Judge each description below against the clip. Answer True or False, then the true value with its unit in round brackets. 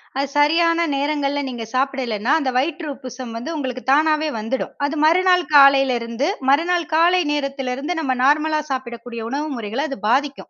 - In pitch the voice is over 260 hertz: True (275 Hz)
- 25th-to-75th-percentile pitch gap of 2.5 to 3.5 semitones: True (3.2 semitones)